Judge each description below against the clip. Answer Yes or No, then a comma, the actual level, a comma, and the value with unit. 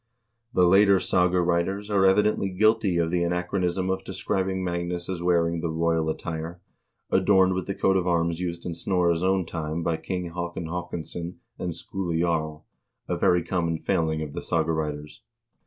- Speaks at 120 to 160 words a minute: No, average, 170 wpm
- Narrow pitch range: Yes, narrow, 2.1 semitones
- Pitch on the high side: No, very low, 85 Hz